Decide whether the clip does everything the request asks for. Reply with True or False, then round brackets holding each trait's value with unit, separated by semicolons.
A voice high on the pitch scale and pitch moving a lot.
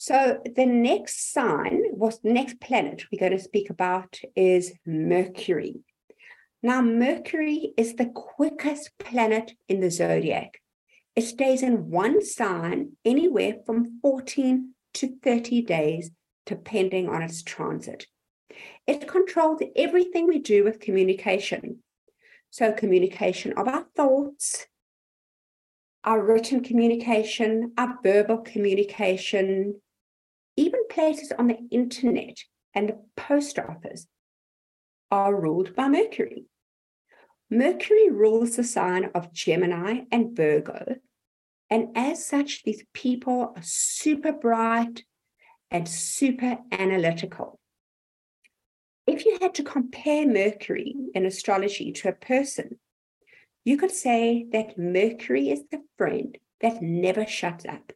True (230 Hz; 6.0 semitones)